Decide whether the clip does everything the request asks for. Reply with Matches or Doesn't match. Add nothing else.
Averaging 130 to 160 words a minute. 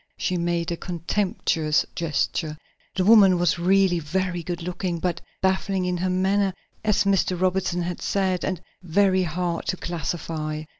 Matches